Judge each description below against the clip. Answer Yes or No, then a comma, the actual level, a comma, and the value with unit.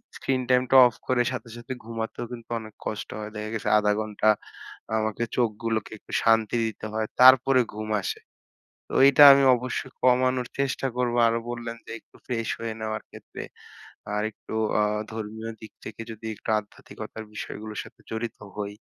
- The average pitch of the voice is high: No, low, 115 Hz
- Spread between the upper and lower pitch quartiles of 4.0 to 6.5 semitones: No, narrow, 2.4 semitones